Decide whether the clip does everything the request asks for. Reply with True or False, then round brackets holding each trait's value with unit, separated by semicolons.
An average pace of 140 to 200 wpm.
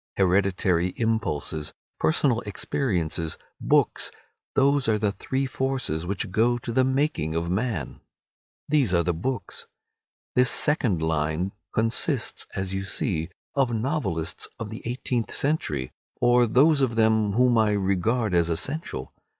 False (130 wpm)